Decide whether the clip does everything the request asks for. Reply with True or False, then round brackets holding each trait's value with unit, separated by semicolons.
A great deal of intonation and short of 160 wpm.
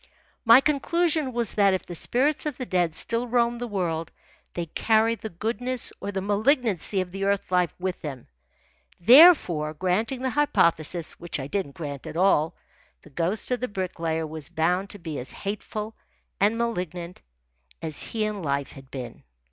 False (6.0 semitones; 170 wpm)